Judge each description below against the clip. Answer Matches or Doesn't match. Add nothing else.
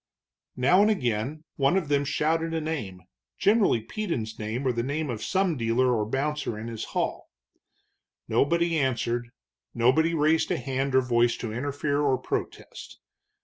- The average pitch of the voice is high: Doesn't match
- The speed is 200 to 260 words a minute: Doesn't match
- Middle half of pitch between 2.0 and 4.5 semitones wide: Doesn't match